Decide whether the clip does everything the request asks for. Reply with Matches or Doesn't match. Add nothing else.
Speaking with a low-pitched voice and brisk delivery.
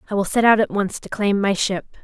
Doesn't match